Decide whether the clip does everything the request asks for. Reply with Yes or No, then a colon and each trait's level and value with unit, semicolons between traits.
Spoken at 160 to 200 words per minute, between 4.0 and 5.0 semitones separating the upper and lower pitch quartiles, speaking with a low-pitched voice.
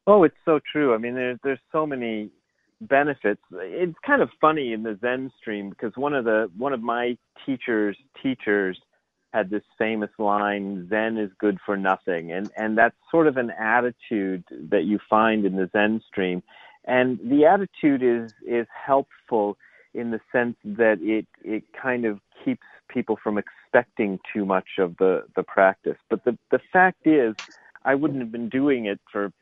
Yes: average, 175 wpm; average, 4.7 semitones; low, 115 Hz